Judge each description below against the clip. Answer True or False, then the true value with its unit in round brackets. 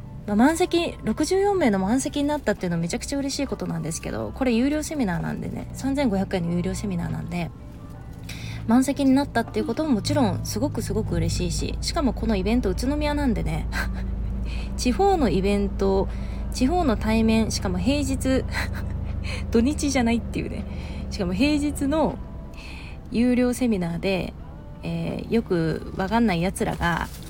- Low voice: False (215 Hz)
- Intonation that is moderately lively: False (8.5 semitones)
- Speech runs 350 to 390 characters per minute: False (340 characters per minute)